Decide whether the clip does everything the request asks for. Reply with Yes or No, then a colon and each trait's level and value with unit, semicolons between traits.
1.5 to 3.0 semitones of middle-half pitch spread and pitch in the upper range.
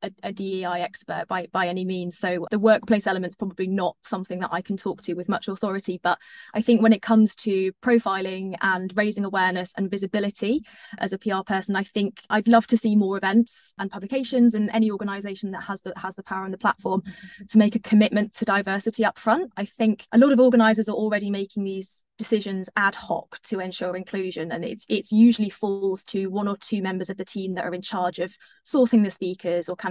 Yes: average, 2.7 semitones; high, 200 Hz